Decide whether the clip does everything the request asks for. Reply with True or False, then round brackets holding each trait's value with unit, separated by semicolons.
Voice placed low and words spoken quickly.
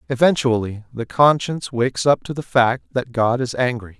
False (125 Hz; 180 wpm)